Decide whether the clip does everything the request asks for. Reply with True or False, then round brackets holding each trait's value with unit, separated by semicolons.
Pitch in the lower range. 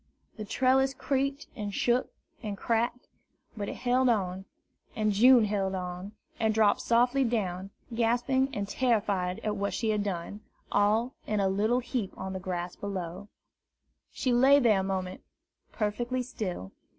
False (215 Hz)